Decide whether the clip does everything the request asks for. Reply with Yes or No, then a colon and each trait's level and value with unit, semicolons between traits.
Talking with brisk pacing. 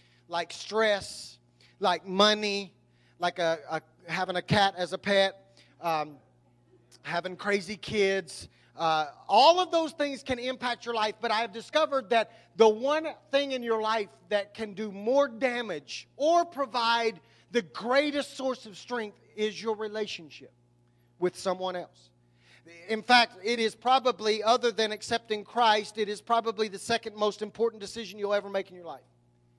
No: average, 160 wpm